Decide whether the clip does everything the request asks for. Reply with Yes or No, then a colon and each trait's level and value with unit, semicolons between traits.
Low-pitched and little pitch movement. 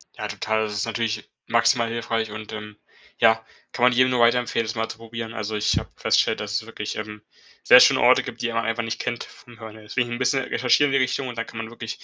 Yes: low, 115 Hz; narrow, 1.5 semitones